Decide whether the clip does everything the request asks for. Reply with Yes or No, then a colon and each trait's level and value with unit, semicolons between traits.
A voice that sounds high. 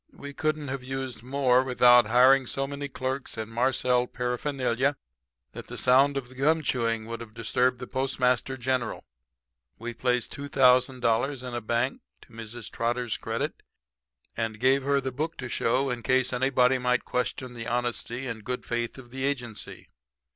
No: low, 125 Hz